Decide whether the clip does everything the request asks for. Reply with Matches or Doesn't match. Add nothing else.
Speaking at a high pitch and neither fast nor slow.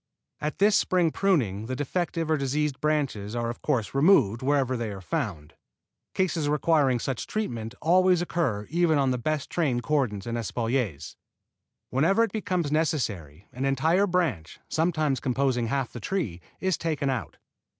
Doesn't match